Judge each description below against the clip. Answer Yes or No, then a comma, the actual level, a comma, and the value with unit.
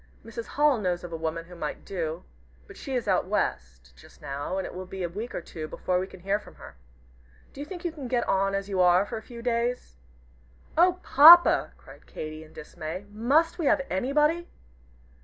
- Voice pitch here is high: Yes, high, 195 Hz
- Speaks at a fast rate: Yes, fast, 215 wpm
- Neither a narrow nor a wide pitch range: No, wide, 7.4 semitones